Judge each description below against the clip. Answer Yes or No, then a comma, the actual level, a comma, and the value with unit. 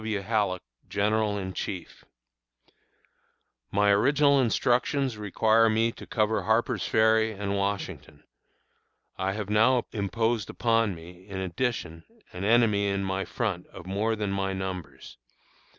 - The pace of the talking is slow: Yes, slow, 130 wpm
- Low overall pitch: Yes, low, 105 Hz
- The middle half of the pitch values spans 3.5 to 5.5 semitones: No, narrow, 2.6 semitones